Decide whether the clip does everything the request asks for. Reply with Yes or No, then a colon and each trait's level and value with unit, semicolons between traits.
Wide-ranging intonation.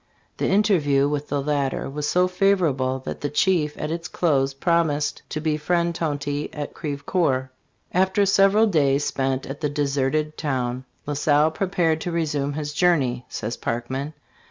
No: average, 3.4 semitones